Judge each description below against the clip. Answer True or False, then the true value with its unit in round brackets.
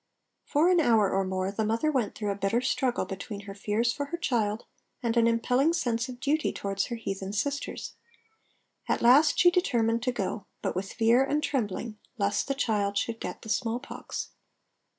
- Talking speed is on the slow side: False (185 wpm)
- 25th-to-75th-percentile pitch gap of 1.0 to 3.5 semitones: False (4.6 semitones)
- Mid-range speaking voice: False (230 Hz)